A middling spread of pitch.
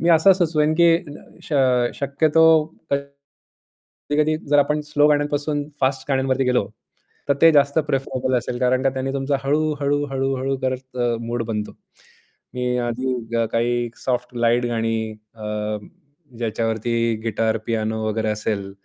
Yes: average, 3.8 semitones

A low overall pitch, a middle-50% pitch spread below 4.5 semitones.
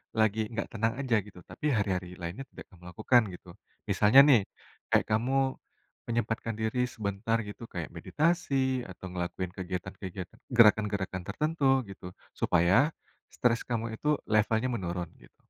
No: low, 110 Hz; average, 4.9 semitones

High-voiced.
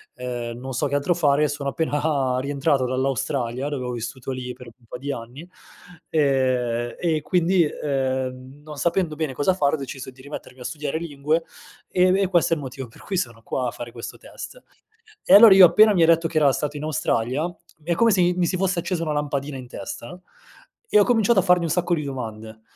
No: medium, 145 Hz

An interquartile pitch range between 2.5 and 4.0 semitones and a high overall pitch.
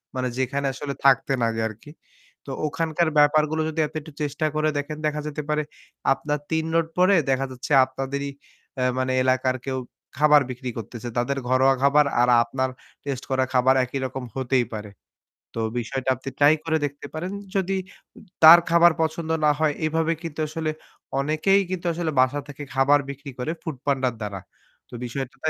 No: average, 3.2 semitones; medium, 140 Hz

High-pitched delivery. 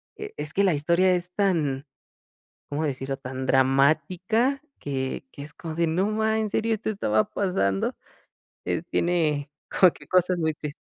No: medium, 160 Hz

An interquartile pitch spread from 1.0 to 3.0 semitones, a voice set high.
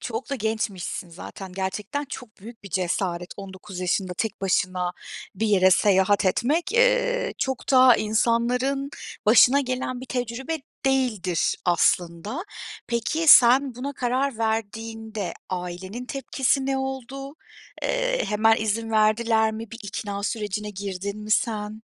No: average, 4.5 semitones; high, 225 Hz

